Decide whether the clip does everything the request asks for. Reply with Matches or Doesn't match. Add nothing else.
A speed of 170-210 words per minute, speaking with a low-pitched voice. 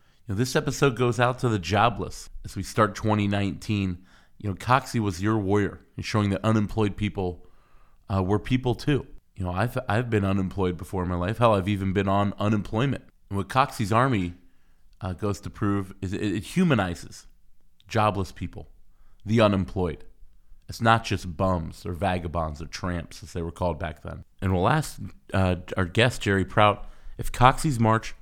Matches